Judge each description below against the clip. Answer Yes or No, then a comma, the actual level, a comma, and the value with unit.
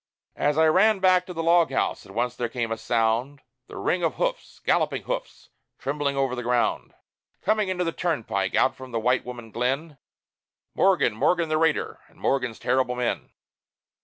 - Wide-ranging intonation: Yes, wide, 5.9 semitones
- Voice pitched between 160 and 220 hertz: No, low, 135 Hz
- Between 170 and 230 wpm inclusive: Yes, average, 180 wpm